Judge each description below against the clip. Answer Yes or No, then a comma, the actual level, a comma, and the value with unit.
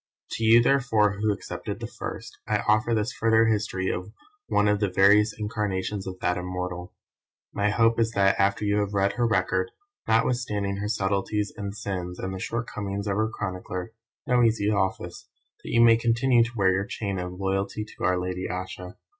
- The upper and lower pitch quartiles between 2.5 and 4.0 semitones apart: Yes, average, 2.8 semitones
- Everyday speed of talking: Yes, average, 180 wpm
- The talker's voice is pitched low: Yes, low, 100 Hz